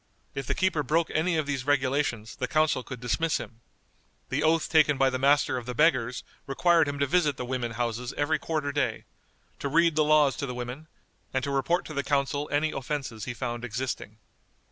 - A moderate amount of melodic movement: Yes, average, 3.4 semitones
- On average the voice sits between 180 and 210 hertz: No, medium, 140 Hz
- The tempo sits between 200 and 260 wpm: Yes, fast, 205 wpm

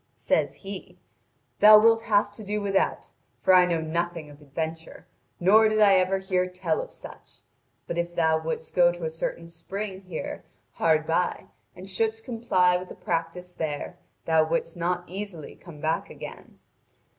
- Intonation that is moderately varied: Yes, average, 3.2 semitones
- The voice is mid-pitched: Yes, medium, 180 Hz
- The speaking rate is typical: Yes, average, 170 wpm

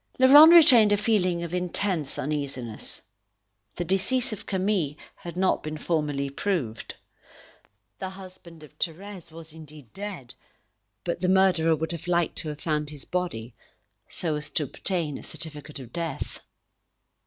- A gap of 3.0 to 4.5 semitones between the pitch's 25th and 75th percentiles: Yes, average, 4.0 semitones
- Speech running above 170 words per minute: No, average, 145 wpm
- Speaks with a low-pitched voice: No, medium, 170 Hz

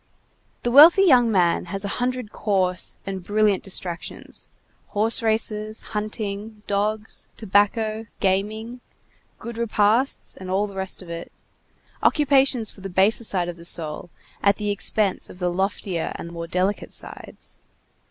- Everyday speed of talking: Yes, average, 145 wpm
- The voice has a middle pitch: No, high, 205 Hz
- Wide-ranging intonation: No, average, 2.8 semitones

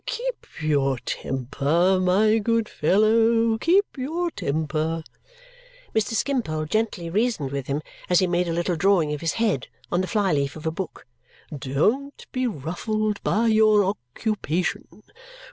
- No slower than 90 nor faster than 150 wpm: Yes, average, 145 wpm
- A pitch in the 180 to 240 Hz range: Yes, medium, 185 Hz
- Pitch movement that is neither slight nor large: No, wide, 6.2 semitones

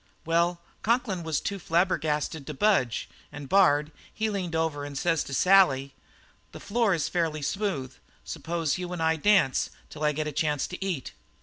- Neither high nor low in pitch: Yes, medium, 165 Hz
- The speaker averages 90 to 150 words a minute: No, average, 175 wpm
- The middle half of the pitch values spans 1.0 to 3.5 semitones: No, average, 4.1 semitones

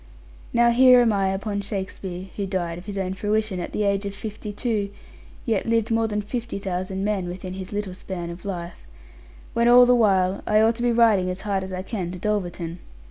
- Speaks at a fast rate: Yes, fast, 215 wpm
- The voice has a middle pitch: No, high, 200 Hz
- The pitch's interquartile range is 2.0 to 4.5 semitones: Yes, average, 2.8 semitones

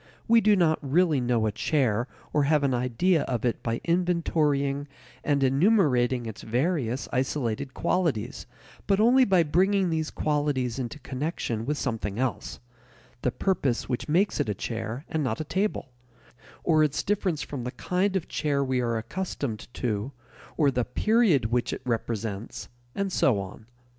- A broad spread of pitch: Yes, wide, 5.8 semitones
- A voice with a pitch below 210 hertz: Yes, medium, 140 Hz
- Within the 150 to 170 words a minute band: Yes, average, 160 wpm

